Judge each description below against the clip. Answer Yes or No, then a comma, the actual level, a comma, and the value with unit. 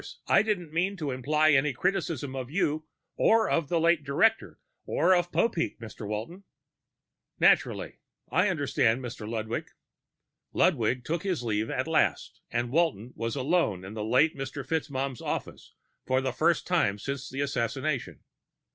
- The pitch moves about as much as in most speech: No, wide, 5.8 semitones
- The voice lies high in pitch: No, medium, 140 Hz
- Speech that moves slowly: No, average, 150 wpm